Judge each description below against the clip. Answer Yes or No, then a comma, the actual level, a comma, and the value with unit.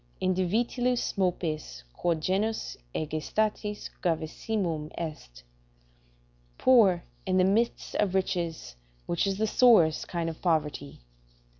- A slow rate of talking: Yes, slow, 110 wpm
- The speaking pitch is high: No, medium, 180 Hz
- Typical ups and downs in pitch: Yes, average, 4.7 semitones